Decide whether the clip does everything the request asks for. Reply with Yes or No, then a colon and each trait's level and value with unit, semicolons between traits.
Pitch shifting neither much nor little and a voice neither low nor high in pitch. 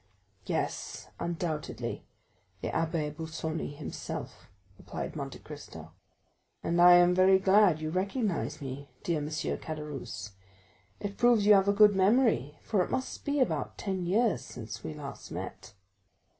Yes: average, 4.9 semitones; medium, 175 Hz